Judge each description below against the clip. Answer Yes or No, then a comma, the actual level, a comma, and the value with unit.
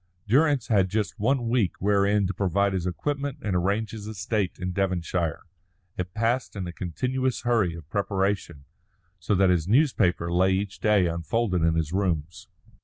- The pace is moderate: Yes, average, 165 wpm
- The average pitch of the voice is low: Yes, low, 100 Hz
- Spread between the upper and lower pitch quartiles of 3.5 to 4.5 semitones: Yes, average, 3.8 semitones